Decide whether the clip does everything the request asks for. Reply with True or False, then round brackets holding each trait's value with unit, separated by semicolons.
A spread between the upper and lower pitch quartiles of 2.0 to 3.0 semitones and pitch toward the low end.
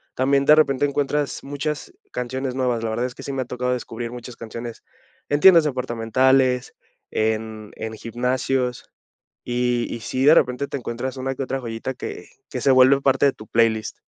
True (2.4 semitones; 125 Hz)